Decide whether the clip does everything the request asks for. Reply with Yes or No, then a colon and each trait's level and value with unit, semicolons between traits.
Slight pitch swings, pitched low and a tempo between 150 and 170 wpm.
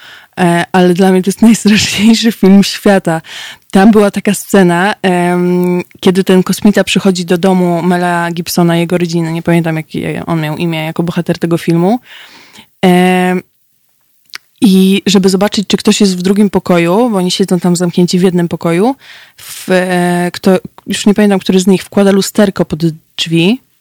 No: narrow, 2.2 semitones; medium, 185 Hz; average, 155 wpm